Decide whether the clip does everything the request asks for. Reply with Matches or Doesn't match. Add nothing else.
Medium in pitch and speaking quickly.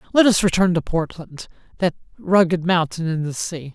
Doesn't match